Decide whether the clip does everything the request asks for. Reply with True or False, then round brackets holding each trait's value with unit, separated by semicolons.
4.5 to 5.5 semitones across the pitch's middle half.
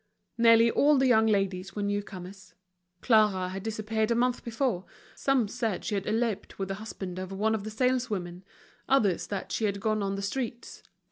False (3.0 semitones)